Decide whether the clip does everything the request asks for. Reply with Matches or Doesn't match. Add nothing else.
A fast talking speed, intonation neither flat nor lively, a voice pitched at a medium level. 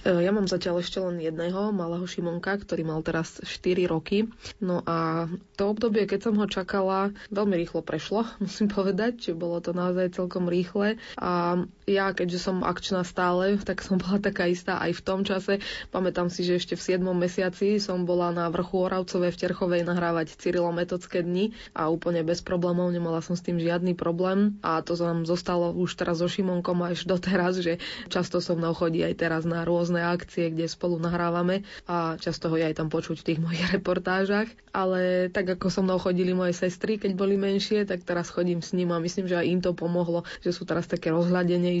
Doesn't match